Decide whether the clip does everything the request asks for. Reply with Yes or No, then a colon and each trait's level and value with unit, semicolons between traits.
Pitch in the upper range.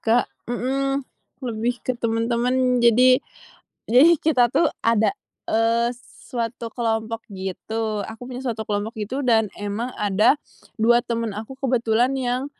Yes: high, 235 Hz